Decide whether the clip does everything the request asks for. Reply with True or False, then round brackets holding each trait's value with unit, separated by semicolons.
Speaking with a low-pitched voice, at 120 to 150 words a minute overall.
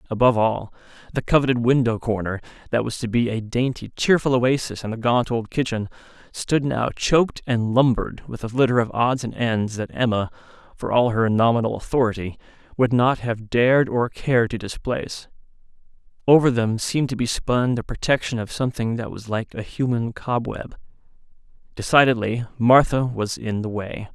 False (120 Hz; 170 wpm)